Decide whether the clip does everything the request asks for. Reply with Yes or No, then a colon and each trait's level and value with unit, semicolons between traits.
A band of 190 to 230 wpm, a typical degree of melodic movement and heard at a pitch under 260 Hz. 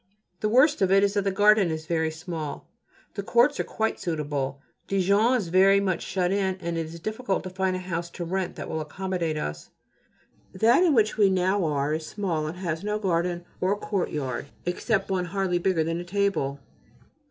Yes: average, 200 wpm; average, 3.4 semitones; medium, 185 Hz